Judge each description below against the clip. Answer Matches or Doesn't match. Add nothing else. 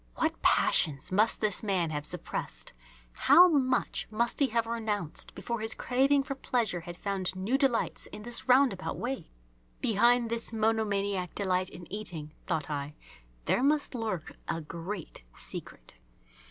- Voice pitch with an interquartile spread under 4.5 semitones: Doesn't match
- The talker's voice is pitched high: Matches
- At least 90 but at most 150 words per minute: Matches